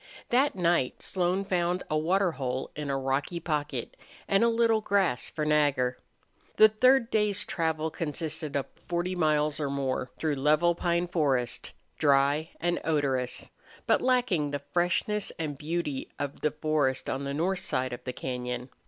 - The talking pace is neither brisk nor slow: Yes, average, 160 wpm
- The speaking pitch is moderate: Yes, medium, 155 Hz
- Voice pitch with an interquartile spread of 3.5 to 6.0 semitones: Yes, average, 4.2 semitones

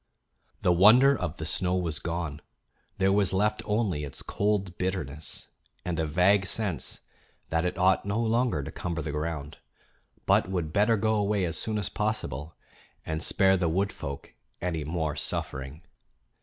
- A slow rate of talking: No, average, 160 wpm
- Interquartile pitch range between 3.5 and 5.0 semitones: Yes, average, 4.3 semitones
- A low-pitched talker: Yes, very low, 90 Hz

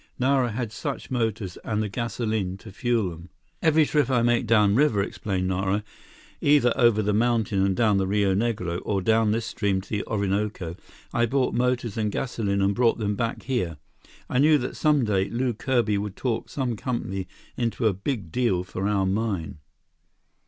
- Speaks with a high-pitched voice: No, low, 110 Hz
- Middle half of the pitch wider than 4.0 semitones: No, average, 3.6 semitones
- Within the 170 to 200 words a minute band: Yes, average, 180 wpm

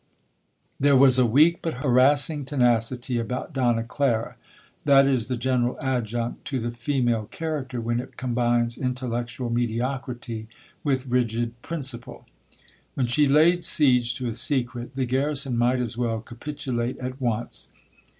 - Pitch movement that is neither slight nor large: No, narrow, 2.3 semitones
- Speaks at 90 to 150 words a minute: Yes, average, 140 wpm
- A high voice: No, low, 125 Hz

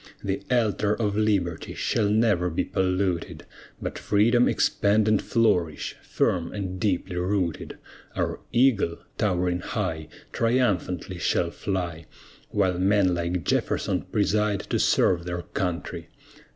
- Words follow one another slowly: Yes, slow, 120 wpm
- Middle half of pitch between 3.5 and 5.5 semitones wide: No, average, 3.1 semitones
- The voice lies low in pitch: Yes, very low, 95 Hz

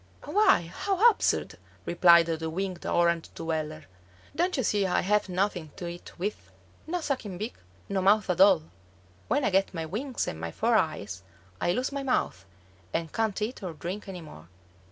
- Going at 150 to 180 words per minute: Yes, average, 175 wpm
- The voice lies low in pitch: No, medium, 185 Hz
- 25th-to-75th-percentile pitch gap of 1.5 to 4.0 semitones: No, average, 4.7 semitones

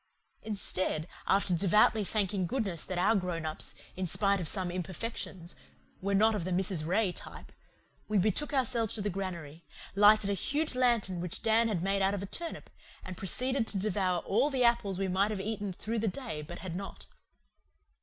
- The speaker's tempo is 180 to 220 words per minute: Yes, average, 185 wpm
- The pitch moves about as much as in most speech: Yes, average, 3.2 semitones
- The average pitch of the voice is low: No, high, 195 Hz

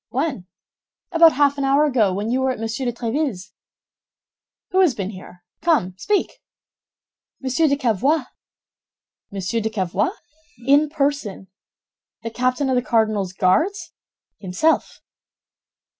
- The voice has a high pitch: Yes, very high, 255 Hz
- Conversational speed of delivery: No, slow, 130 wpm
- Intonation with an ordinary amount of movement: No, wide, 6.0 semitones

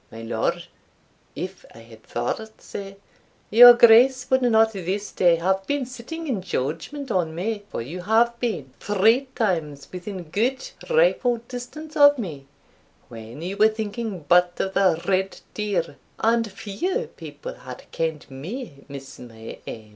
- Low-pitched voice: No, high, 200 Hz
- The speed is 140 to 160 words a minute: Yes, average, 150 wpm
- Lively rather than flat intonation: Yes, wide, 6.6 semitones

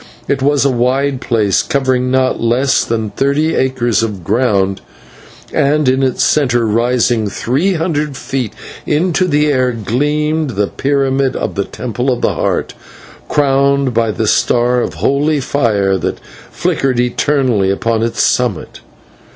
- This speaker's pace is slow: No, average, 145 wpm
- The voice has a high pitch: No, low, 130 Hz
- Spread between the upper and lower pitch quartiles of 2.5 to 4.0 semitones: Yes, average, 3.3 semitones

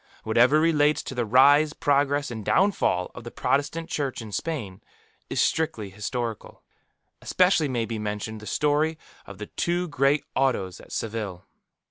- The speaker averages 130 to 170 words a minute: Yes, average, 150 wpm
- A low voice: Yes, low, 130 Hz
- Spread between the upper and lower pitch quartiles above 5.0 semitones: Yes, wide, 5.5 semitones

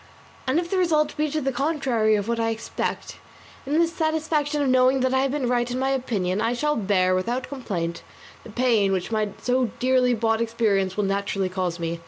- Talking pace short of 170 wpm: No, fast, 205 wpm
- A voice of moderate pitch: No, high, 245 Hz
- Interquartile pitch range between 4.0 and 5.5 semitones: Yes, average, 5.0 semitones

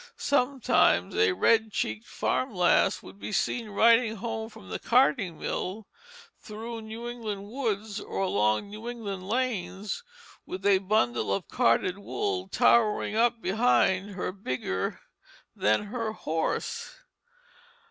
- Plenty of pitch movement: No, average, 3.8 semitones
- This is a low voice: No, high, 215 Hz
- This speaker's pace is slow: Yes, slow, 125 wpm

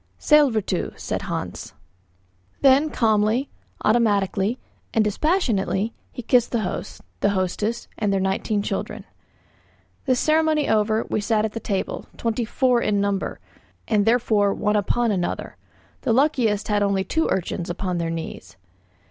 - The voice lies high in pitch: Yes, high, 215 Hz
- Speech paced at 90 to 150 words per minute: Yes, slow, 135 wpm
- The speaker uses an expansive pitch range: No, average, 3.3 semitones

